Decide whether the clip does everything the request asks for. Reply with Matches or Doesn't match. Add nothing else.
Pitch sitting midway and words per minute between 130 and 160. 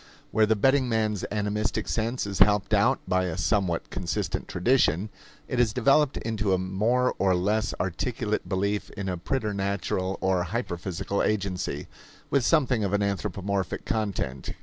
Doesn't match